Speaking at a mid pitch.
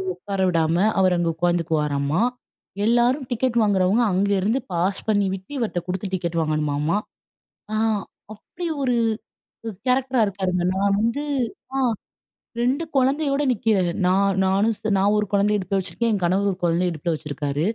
No: high, 195 Hz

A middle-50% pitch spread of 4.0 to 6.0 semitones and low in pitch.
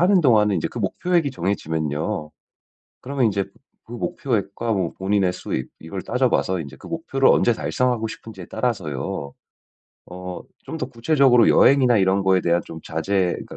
Yes: wide, 5.7 semitones; low, 105 Hz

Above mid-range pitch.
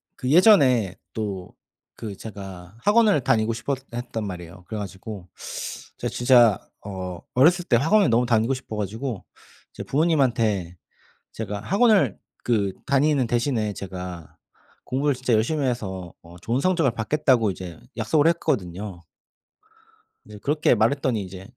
No: low, 115 Hz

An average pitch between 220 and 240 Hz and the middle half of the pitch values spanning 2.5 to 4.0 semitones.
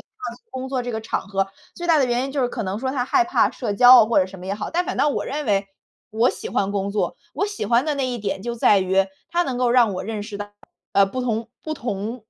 No: high, 235 Hz; average, 4.4 semitones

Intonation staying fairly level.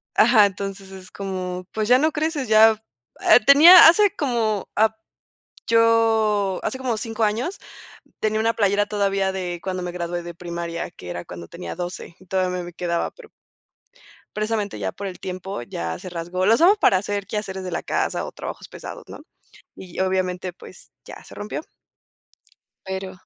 No: average, 3.5 semitones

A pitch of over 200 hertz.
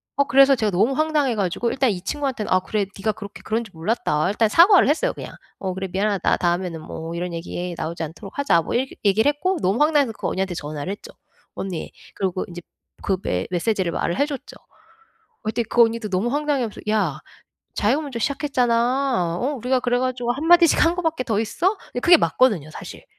Yes: high, 225 Hz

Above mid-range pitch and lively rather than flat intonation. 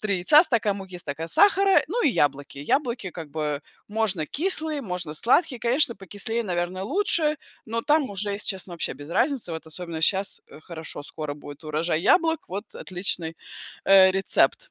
Yes: high, 195 Hz; wide, 7.7 semitones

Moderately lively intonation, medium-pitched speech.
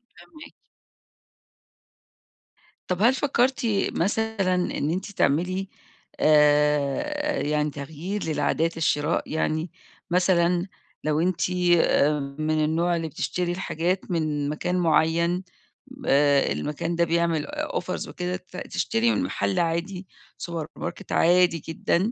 Yes: average, 3.1 semitones; medium, 170 Hz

